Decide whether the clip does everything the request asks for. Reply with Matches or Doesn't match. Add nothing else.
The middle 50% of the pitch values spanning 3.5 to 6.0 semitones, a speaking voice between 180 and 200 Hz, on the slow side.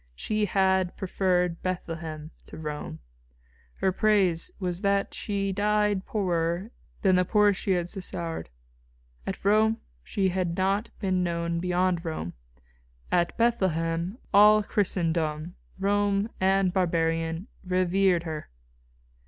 Doesn't match